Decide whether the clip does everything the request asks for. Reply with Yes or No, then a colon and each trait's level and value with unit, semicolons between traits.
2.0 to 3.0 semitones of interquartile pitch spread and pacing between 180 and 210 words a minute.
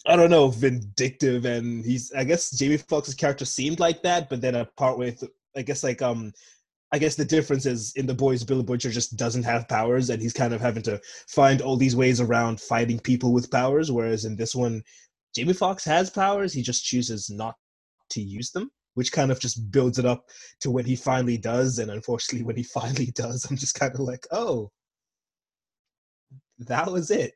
Yes: narrow, 2.6 semitones; fast, 205 wpm